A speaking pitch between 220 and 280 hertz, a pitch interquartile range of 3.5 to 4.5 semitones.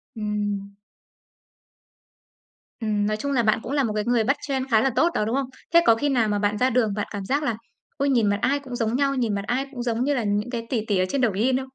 Yes: high, 230 Hz; average, 3.9 semitones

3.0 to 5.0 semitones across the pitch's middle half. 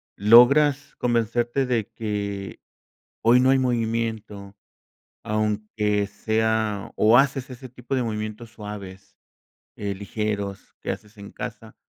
No: narrow, 2.6 semitones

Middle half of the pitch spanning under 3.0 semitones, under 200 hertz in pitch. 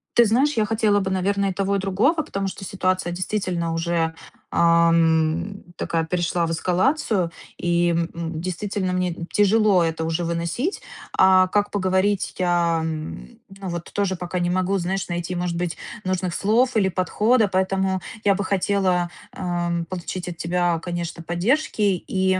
Yes: narrow, 2.5 semitones; medium, 185 Hz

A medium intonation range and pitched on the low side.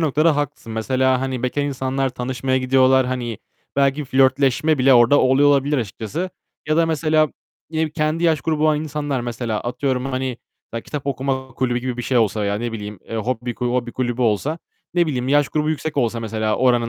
Yes: average, 3.2 semitones; low, 130 Hz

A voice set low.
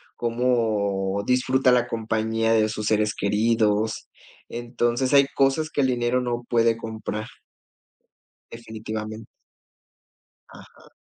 Yes: low, 115 Hz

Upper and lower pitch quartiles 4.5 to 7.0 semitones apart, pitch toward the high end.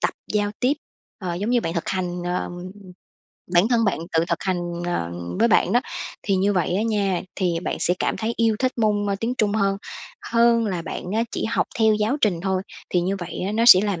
No: average, 3.8 semitones; high, 200 Hz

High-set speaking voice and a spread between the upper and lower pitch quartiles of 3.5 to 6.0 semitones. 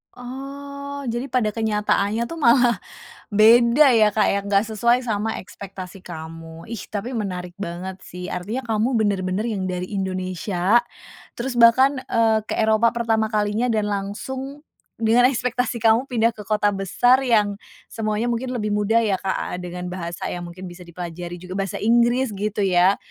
Yes: high, 215 Hz; average, 4.0 semitones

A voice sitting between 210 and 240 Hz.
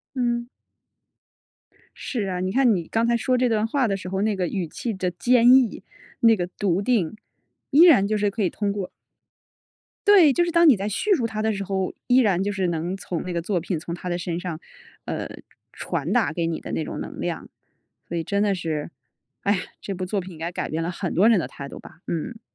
No: high, 200 Hz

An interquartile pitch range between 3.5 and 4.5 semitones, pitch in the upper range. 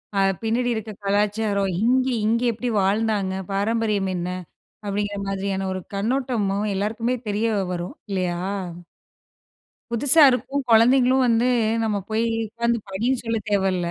No: average, 3.0 semitones; high, 215 Hz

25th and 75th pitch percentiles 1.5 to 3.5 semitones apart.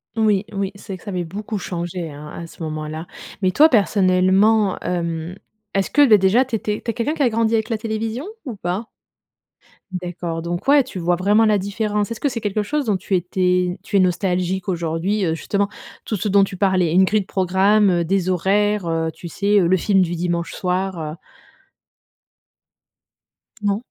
Yes: average, 3.1 semitones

